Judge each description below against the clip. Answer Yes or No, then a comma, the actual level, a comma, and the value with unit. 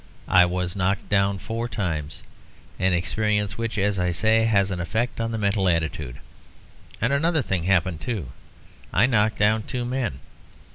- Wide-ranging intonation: No, average, 3.9 semitones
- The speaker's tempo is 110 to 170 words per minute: Yes, average, 160 wpm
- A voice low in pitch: Yes, low, 100 Hz